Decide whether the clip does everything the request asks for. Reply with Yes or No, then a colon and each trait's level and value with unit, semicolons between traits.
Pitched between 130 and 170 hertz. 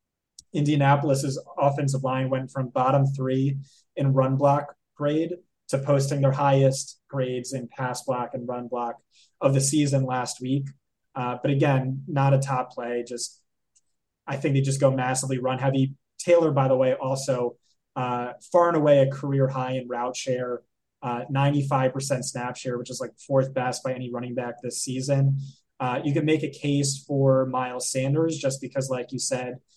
Yes: low, 135 Hz